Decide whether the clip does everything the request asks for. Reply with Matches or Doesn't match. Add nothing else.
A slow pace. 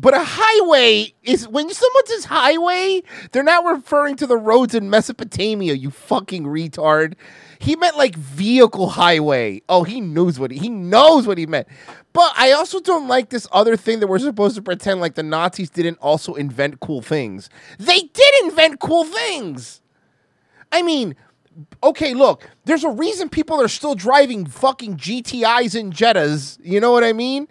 Doesn't match